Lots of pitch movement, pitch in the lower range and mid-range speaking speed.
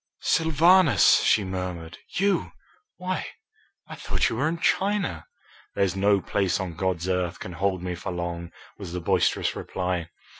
Yes: wide, 8.5 semitones; very low, 95 Hz; average, 150 wpm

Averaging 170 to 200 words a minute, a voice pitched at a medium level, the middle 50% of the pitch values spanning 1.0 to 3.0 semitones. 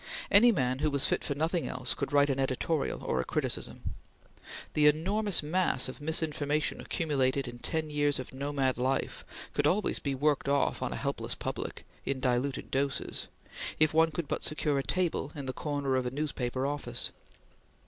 Yes: average, 180 wpm; medium, 145 Hz; narrow, 2.6 semitones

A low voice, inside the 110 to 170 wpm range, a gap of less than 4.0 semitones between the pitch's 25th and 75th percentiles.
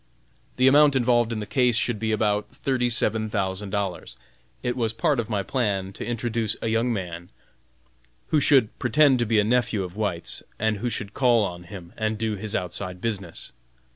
No: low, 110 Hz; average, 190 wpm; average, 3.3 semitones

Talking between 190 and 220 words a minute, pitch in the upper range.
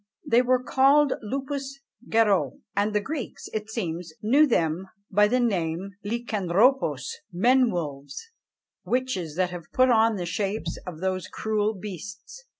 No: average, 150 wpm; high, 210 Hz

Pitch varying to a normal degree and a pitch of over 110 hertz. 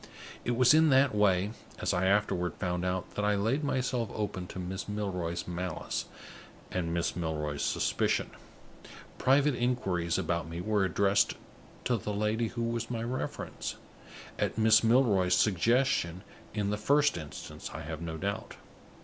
No: average, 4.7 semitones; low, 100 Hz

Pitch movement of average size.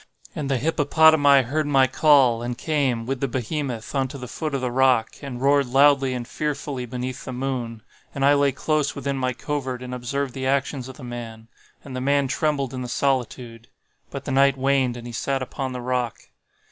No: narrow, 2.1 semitones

